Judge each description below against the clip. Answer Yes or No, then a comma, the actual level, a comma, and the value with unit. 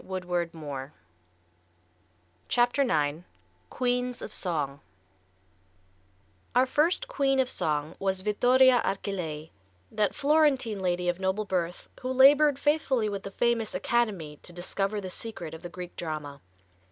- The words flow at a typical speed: No, slow, 130 wpm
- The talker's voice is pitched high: Yes, high, 195 Hz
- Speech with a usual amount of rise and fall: No, wide, 6.5 semitones